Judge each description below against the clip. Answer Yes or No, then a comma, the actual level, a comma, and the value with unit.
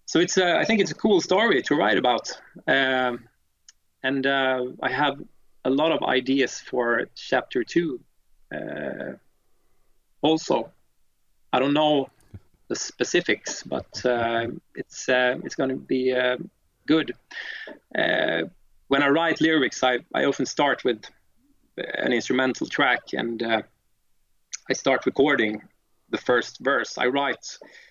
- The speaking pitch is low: Yes, low, 130 Hz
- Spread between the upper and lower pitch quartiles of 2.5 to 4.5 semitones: No, average, 5.1 semitones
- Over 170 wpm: No, average, 140 wpm